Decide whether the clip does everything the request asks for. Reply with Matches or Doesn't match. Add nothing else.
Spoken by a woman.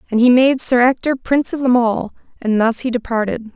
Matches